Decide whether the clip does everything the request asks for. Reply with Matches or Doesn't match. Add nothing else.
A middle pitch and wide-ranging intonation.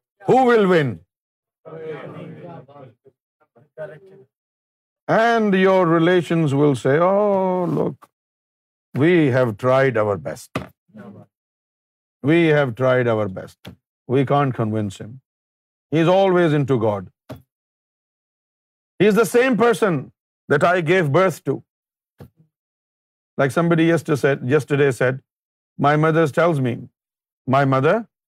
Doesn't match